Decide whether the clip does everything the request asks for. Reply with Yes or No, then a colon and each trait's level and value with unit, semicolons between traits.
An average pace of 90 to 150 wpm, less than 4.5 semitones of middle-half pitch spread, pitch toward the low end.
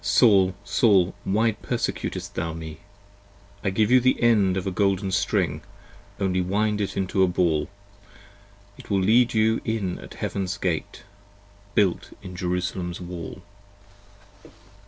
Yes: average, 140 wpm; average, 2.7 semitones; very low, 95 Hz